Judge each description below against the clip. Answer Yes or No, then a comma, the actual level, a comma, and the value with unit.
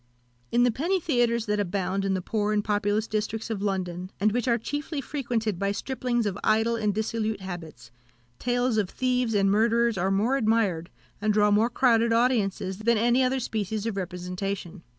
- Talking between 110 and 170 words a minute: No, average, 180 wpm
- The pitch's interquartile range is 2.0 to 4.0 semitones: Yes, average, 3.1 semitones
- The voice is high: Yes, high, 215 Hz